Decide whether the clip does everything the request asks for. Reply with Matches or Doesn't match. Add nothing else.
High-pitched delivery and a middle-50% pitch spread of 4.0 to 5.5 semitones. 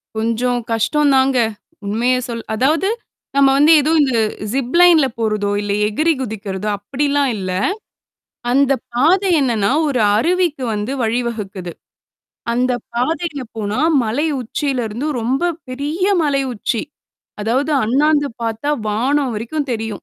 Matches